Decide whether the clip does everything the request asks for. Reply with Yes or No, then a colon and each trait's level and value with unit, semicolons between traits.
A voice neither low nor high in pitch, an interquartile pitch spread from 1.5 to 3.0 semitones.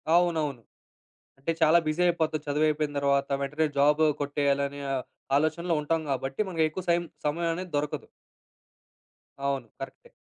Yes: medium, 150 Hz; average, 2.7 semitones